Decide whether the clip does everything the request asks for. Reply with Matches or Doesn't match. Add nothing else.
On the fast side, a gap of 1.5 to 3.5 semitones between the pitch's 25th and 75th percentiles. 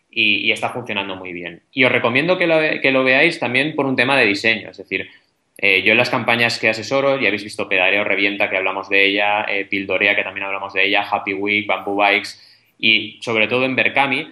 Doesn't match